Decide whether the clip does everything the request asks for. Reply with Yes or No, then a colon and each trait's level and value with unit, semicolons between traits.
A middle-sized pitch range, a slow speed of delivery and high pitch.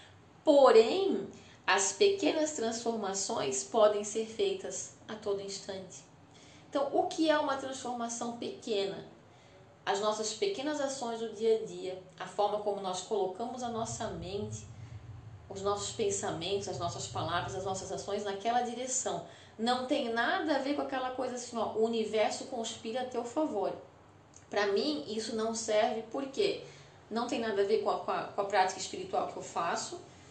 No: average, 4.4 semitones; average, 160 wpm; high, 220 Hz